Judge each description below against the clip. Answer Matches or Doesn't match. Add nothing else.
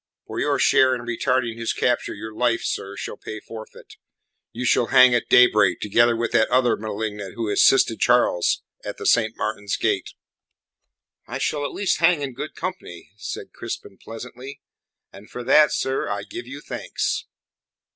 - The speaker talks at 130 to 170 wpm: Matches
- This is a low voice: Matches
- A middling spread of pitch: Matches